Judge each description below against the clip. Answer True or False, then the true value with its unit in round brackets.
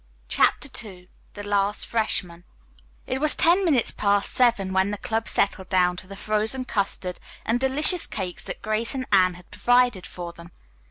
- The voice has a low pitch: False (205 Hz)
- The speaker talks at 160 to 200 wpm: True (170 wpm)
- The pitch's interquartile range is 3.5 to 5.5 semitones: True (4.6 semitones)